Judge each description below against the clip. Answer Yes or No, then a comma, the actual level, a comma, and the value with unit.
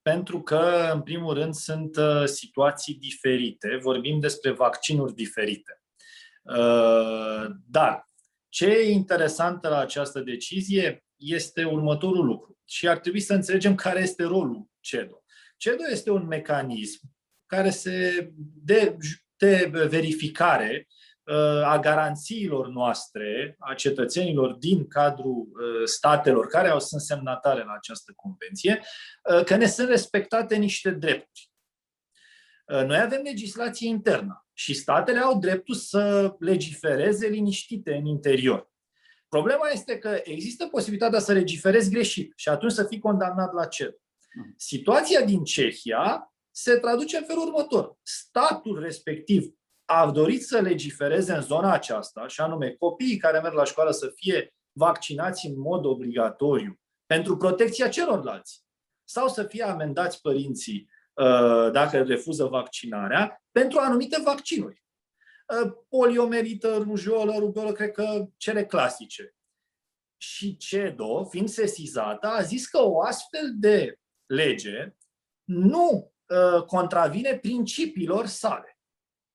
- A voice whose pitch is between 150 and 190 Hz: Yes, medium, 185 Hz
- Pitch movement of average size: No, wide, 6.5 semitones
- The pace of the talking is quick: No, slow, 115 wpm